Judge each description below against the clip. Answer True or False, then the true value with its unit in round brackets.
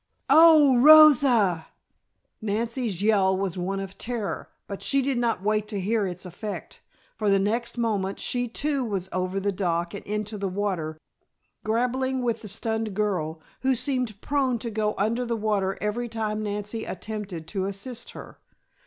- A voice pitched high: True (215 Hz)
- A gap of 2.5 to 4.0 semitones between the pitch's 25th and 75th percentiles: True (3.6 semitones)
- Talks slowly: False (160 wpm)